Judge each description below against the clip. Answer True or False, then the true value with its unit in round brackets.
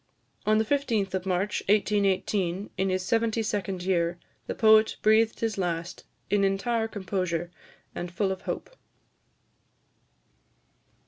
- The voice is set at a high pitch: True (195 Hz)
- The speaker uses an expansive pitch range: False (2.8 semitones)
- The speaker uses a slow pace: True (125 wpm)